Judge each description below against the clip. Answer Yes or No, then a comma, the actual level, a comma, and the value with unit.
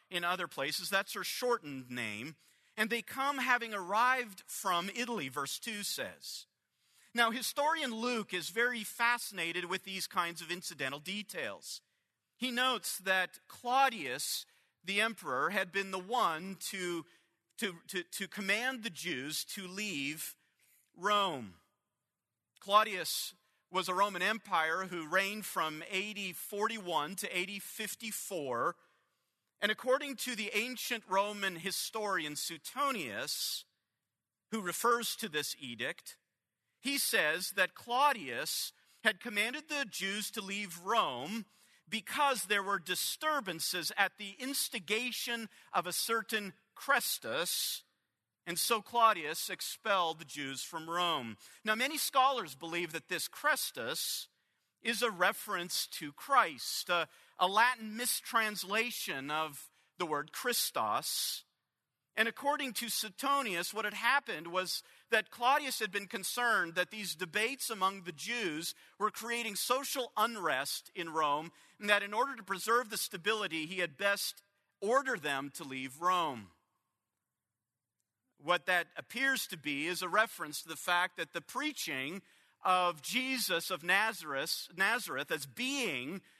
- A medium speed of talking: No, slow, 130 wpm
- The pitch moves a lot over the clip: No, average, 5.0 semitones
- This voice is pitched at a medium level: No, high, 200 Hz